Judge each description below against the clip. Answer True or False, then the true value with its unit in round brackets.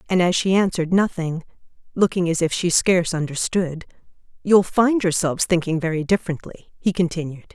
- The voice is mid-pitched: True (175 Hz)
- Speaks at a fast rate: False (150 wpm)